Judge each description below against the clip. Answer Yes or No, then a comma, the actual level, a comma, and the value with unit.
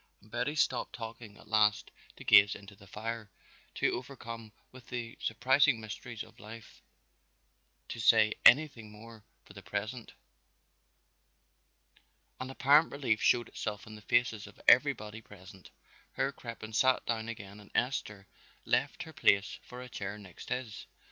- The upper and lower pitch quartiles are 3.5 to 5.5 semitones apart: No, average, 2.7 semitones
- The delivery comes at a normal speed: Yes, average, 150 wpm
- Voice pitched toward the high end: No, low, 110 Hz